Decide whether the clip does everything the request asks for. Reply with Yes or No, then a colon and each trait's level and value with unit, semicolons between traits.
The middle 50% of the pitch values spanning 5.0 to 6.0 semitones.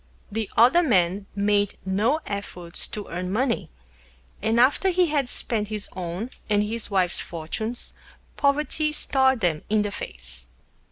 Yes: wide, 5.5 semitones